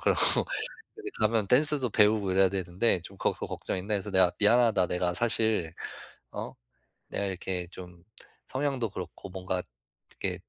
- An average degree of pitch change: Yes, average, 3.7 semitones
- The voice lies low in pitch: Yes, low, 100 Hz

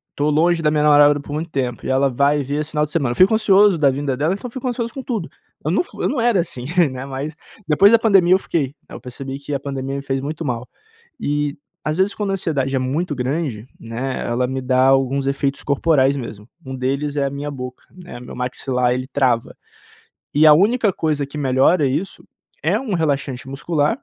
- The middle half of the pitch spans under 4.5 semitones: Yes, average, 3.9 semitones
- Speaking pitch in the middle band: Yes, medium, 145 Hz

